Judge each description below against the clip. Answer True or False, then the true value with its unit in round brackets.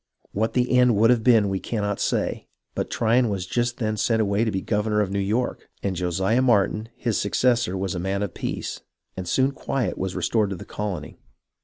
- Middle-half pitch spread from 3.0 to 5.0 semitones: True (3.4 semitones)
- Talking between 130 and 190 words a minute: False (205 wpm)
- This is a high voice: False (105 Hz)